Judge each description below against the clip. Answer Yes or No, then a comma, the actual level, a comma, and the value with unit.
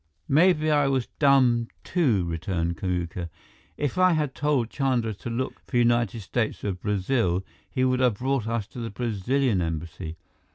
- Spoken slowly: No, average, 160 wpm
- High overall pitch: No, low, 120 Hz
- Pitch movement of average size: No, wide, 6.1 semitones